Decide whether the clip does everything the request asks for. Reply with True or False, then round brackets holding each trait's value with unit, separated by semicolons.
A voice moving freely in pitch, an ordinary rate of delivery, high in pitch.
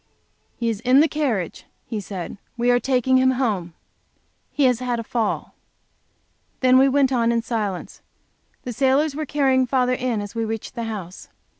False (2.8 semitones; 175 wpm; 245 Hz)